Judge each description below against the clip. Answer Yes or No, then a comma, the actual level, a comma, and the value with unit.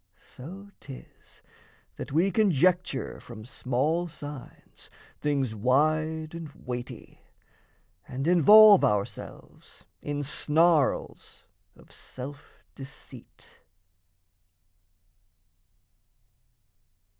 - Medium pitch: Yes, medium, 150 Hz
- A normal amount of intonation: Yes, average, 4.3 semitones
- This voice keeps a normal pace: No, slow, 70 wpm